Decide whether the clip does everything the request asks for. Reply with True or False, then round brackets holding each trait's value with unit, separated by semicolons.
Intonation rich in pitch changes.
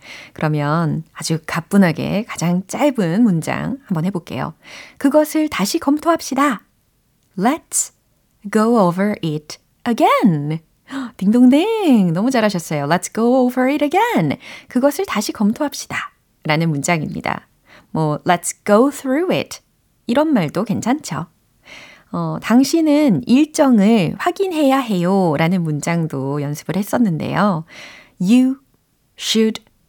True (8.3 semitones)